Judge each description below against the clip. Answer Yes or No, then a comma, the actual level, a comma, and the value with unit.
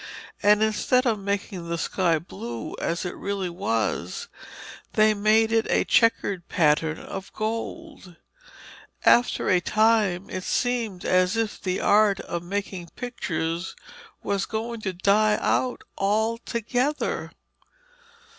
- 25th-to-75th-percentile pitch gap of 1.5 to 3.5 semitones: No, average, 3.9 semitones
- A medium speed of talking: No, slow, 120 wpm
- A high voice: Yes, high, 200 Hz